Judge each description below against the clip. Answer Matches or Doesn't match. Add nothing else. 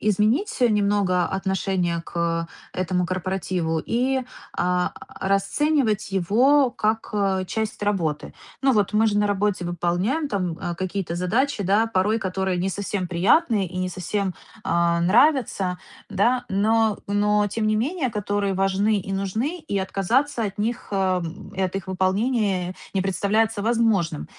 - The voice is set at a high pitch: Matches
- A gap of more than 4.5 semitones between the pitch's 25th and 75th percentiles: Doesn't match